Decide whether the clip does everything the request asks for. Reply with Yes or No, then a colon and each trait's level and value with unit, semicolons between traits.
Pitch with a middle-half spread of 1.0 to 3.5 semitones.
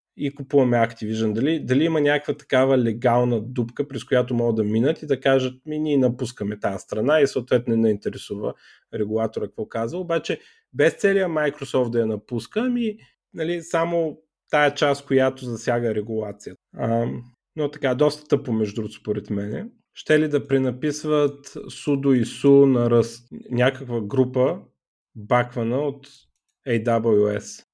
No: average, 4.1 semitones